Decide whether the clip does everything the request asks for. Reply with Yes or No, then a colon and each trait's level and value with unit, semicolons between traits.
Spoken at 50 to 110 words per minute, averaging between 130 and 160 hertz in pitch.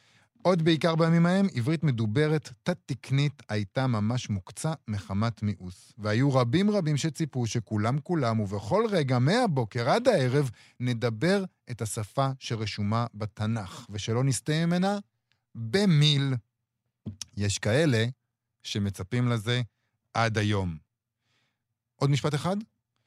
No: average, 105 wpm; low, 120 Hz